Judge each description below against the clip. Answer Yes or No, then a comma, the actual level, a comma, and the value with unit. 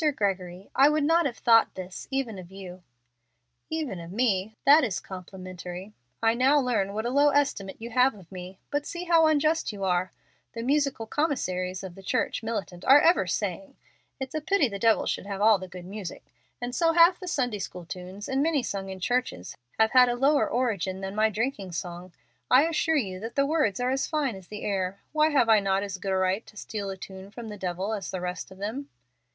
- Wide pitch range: Yes, wide, 6.3 semitones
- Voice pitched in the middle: No, high, 215 Hz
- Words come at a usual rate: No, fast, 220 wpm